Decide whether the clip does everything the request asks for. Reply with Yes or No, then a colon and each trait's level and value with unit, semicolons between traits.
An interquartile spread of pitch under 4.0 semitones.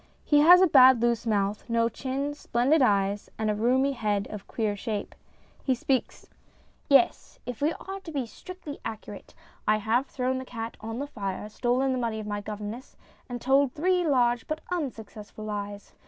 No: average, 4.5 semitones